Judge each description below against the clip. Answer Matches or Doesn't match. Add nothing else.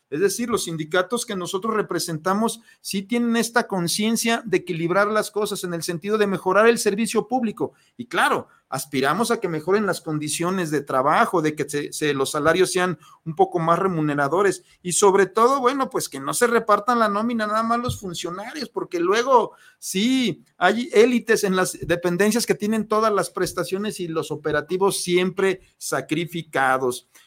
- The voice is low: Doesn't match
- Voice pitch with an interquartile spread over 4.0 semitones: Matches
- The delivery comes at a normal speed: Matches